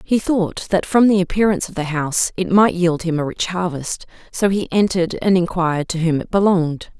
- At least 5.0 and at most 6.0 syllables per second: Yes, 5.5 syllables/s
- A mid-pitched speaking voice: Yes, medium, 180 Hz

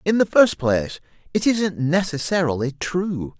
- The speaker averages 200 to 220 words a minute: No, average, 140 wpm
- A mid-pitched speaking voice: Yes, medium, 165 Hz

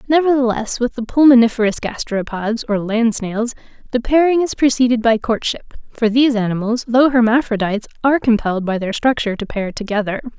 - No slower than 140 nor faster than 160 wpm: Yes, average, 155 wpm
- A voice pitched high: Yes, high, 235 Hz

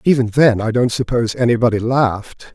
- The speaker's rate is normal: Yes, average, 165 wpm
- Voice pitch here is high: No, low, 120 Hz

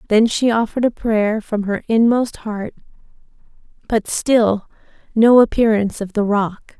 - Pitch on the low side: No, high, 220 Hz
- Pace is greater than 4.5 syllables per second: No, 4.4 syllables/s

